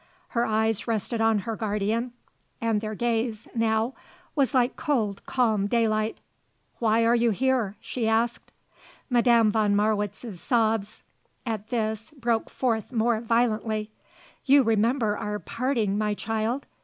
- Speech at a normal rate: No, slow, 130 wpm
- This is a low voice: No, high, 225 Hz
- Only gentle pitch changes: Yes, narrow, 1.7 semitones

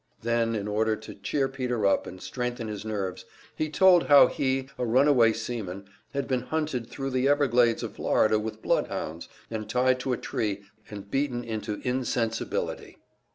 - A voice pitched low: Yes, low, 120 Hz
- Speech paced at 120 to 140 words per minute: No, average, 165 wpm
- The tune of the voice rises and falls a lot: No, average, 3.5 semitones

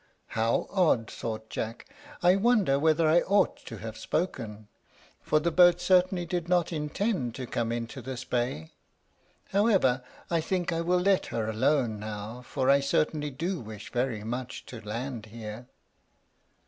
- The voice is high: No, low, 135 Hz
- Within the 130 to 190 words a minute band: Yes, average, 155 wpm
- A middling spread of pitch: No, wide, 7.2 semitones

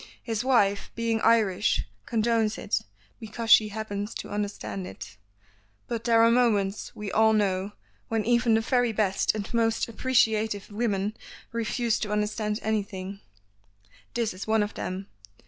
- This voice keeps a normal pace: Yes, average, 145 wpm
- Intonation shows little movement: Yes, narrow, 2.1 semitones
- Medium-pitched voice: No, high, 215 Hz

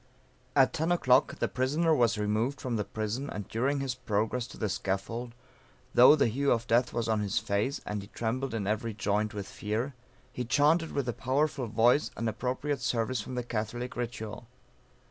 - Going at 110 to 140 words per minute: No, average, 185 wpm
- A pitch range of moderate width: Yes, average, 3.5 semitones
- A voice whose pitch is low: Yes, low, 120 Hz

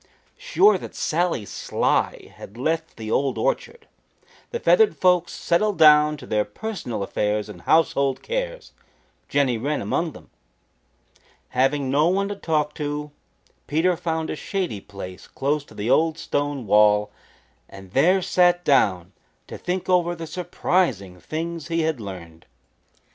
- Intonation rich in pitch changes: Yes, wide, 7.4 semitones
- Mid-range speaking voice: Yes, medium, 150 Hz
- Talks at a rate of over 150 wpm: No, average, 145 wpm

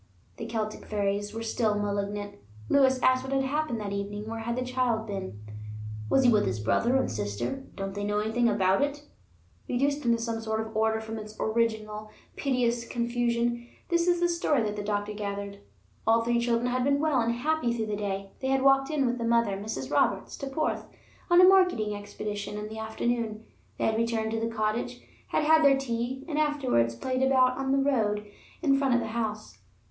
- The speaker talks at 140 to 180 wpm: No, fast, 205 wpm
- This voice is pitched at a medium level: No, high, 230 Hz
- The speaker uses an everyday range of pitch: Yes, average, 3.8 semitones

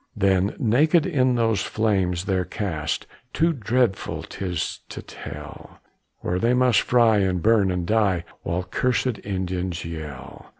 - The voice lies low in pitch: Yes, low, 100 Hz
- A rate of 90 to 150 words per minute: Yes, slow, 135 wpm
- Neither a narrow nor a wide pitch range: Yes, average, 4.5 semitones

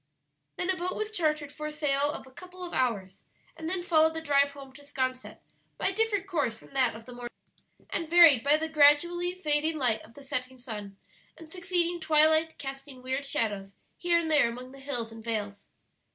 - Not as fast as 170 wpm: No, fast, 205 wpm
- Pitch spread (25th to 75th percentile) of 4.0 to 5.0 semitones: Yes, average, 4.4 semitones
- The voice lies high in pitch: Yes, very high, 290 Hz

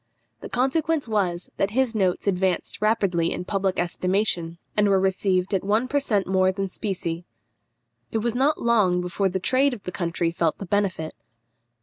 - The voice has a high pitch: Yes, high, 195 Hz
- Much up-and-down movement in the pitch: No, average, 3.4 semitones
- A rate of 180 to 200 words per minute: No, average, 170 wpm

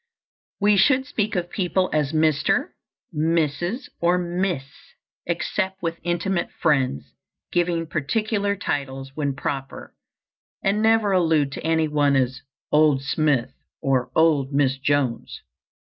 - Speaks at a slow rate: Yes, slow, 120 wpm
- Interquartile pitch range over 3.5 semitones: Yes, average, 4.8 semitones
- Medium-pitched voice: Yes, medium, 160 Hz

